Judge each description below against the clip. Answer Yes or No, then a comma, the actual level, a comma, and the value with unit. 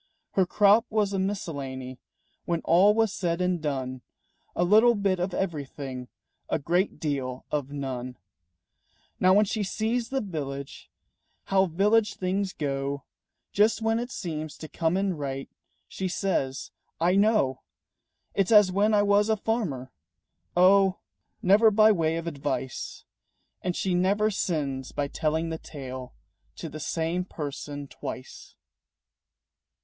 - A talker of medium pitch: Yes, medium, 175 Hz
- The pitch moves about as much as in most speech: No, wide, 6.1 semitones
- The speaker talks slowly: No, average, 145 wpm